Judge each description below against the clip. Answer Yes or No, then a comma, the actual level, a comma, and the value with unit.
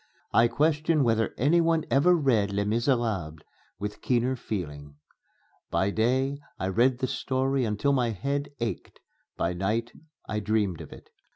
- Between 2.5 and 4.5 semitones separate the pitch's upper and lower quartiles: No, average, 4.9 semitones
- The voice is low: Yes, low, 115 Hz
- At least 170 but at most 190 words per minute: No, average, 150 wpm